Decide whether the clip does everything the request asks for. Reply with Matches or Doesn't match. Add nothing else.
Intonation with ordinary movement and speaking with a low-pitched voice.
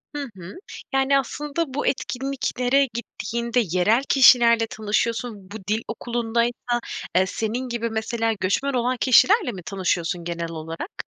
Doesn't match